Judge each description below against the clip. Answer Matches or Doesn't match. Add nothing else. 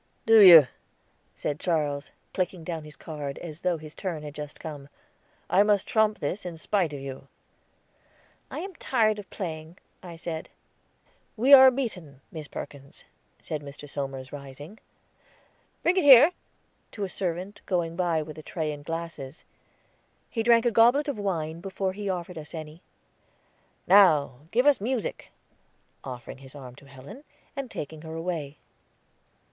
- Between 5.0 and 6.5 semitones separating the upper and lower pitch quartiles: Matches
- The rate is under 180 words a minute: Matches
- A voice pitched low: Doesn't match